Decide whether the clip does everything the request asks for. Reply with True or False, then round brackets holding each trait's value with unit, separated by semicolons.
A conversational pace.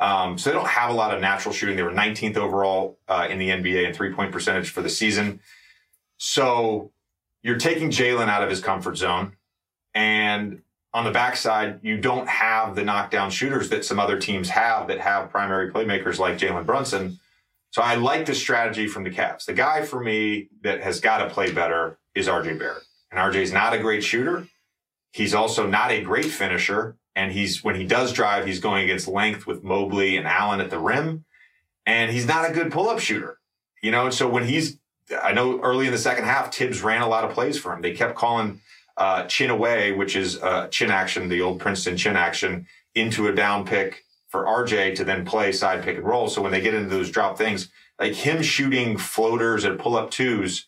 False (215 wpm)